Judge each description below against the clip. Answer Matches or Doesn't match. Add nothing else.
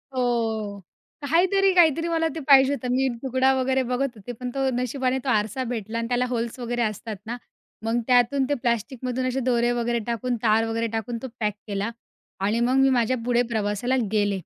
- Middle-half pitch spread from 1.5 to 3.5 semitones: Matches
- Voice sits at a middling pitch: Doesn't match